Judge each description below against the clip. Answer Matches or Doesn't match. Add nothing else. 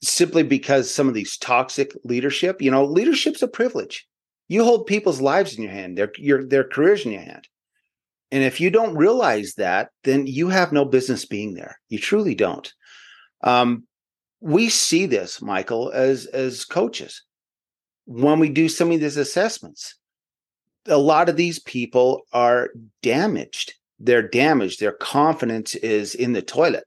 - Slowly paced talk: Doesn't match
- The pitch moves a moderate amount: Doesn't match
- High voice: Doesn't match